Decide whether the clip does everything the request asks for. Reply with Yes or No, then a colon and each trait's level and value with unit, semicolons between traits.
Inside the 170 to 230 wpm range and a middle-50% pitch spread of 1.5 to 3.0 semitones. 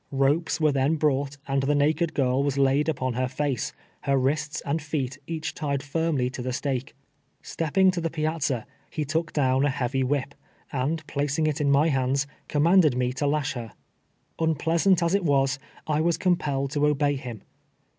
Yes: average, 185 wpm; average, 2.7 semitones